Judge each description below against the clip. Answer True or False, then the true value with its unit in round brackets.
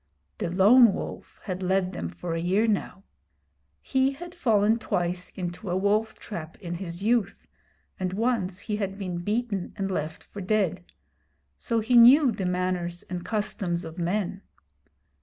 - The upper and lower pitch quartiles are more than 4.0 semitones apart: False (3.5 semitones)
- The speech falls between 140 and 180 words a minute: True (160 wpm)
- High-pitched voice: True (195 Hz)